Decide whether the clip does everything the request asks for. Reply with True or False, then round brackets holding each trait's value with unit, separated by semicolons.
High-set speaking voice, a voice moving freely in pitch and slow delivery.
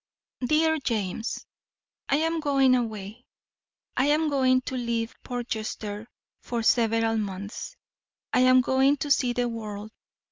False (245 Hz; 3.2 semitones; 130 wpm)